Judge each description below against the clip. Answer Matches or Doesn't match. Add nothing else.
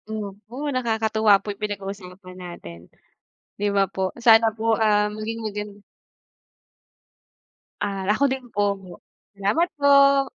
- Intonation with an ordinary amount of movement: Doesn't match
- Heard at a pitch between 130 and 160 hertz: Doesn't match